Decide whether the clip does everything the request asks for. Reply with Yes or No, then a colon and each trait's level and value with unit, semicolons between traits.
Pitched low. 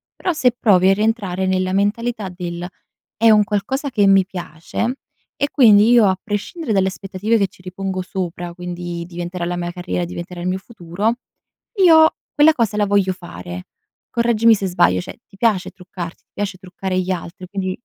No: high, 190 Hz